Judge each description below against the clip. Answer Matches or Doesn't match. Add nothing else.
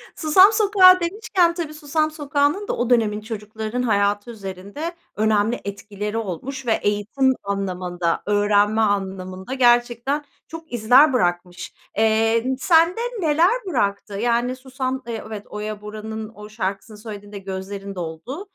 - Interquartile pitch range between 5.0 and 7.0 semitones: Matches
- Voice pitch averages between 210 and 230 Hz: Matches